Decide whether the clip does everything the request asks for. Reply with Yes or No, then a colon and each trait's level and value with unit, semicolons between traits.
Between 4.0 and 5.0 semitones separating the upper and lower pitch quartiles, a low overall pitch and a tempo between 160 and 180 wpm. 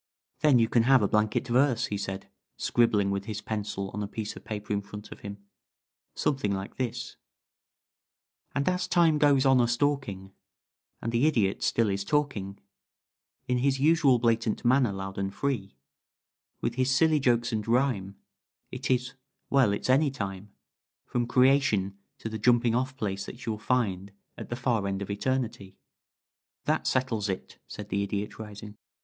Yes: average, 4.4 semitones; low, 115 Hz; average, 170 wpm